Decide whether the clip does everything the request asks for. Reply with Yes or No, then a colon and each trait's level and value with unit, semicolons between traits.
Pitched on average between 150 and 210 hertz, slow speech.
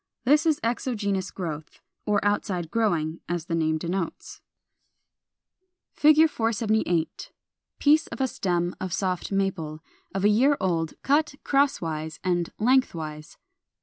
Yes: high, 190 Hz; slow, 125 wpm